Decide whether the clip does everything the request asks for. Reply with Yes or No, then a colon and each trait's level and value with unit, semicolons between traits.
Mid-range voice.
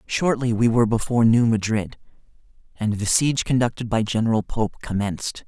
No: low, 115 Hz